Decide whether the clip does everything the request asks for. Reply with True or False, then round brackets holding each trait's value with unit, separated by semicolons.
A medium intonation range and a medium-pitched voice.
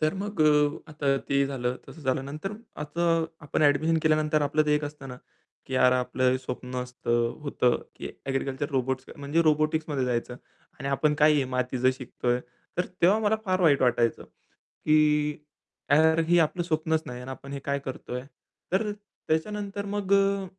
True (3.6 semitones; 145 Hz)